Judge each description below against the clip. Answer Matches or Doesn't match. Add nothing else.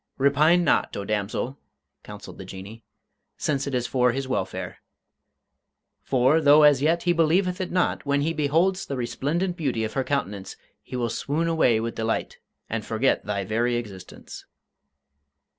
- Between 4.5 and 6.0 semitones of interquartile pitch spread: Matches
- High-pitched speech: Doesn't match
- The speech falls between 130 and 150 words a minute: Doesn't match